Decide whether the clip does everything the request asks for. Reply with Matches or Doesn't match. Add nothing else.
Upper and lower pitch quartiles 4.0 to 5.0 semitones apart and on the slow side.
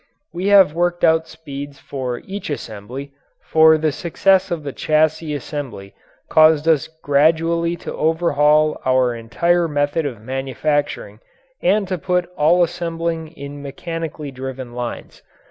Doesn't match